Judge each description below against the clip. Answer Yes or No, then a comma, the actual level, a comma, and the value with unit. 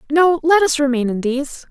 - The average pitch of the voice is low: No, very high, 290 Hz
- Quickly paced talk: Yes, fast, 210 wpm